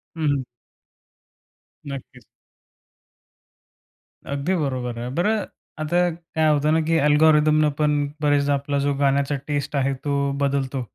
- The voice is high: No, medium, 145 Hz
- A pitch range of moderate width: No, narrow, 1.8 semitones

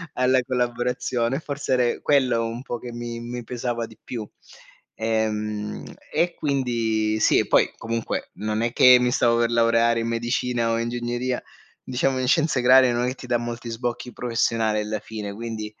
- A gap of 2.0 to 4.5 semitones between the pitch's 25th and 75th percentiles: No, narrow, 1.6 semitones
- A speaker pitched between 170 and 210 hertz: No, low, 120 Hz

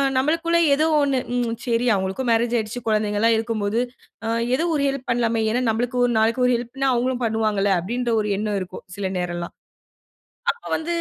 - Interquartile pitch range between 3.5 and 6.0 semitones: No, average, 3.1 semitones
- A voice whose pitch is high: Yes, high, 230 Hz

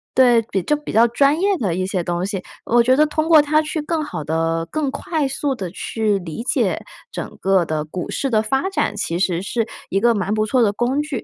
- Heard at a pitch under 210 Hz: No, high, 230 Hz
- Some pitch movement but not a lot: No, wide, 7.7 semitones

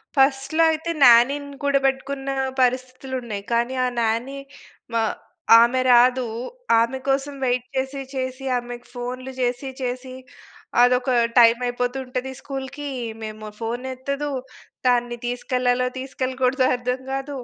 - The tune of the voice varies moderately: No, narrow, 1.7 semitones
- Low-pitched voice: No, very high, 255 Hz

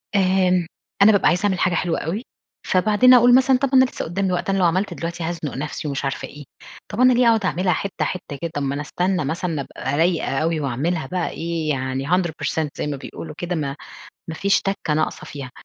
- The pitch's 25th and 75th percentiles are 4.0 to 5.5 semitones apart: Yes, average, 4.4 semitones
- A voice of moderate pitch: Yes, medium, 170 Hz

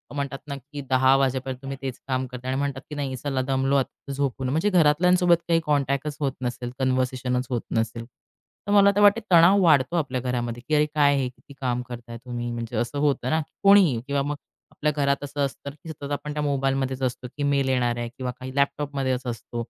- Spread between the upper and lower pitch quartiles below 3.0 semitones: Yes, narrow, 2.4 semitones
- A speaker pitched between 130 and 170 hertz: Yes, low, 135 Hz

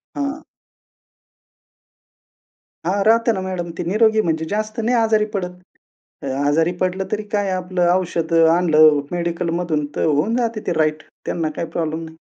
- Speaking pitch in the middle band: Yes, medium, 180 Hz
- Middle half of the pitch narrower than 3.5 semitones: No, average, 4.8 semitones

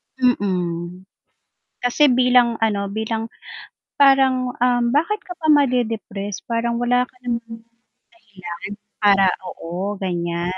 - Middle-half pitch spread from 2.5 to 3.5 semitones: No, average, 4.2 semitones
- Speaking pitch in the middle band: No, high, 230 Hz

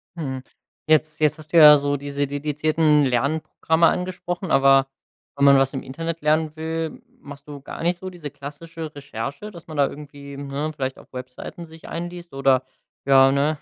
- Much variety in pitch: No, average, 2.7 semitones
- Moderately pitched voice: Yes, medium, 150 Hz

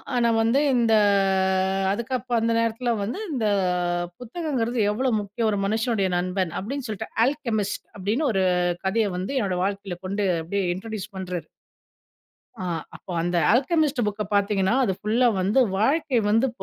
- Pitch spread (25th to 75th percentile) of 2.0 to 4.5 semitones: Yes, average, 3.9 semitones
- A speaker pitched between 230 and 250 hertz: No, high, 220 Hz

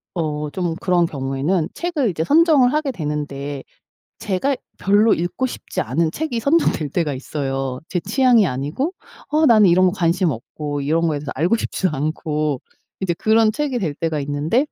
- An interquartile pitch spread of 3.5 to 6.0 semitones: No, wide, 7.4 semitones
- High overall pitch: No, medium, 170 Hz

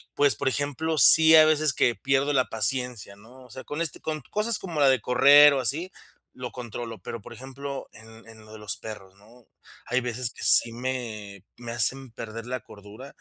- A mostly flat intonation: No, average, 4.0 semitones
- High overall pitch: No, low, 125 Hz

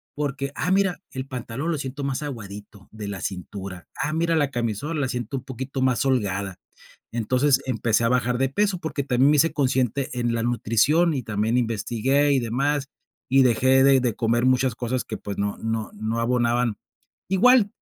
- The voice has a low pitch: Yes, low, 125 Hz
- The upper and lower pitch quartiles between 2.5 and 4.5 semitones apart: Yes, average, 3.5 semitones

